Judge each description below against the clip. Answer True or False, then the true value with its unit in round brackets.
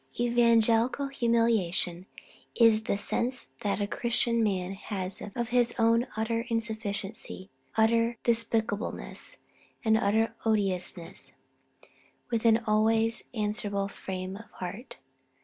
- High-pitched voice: True (225 Hz)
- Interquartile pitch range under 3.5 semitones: True (2.6 semitones)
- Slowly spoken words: True (105 wpm)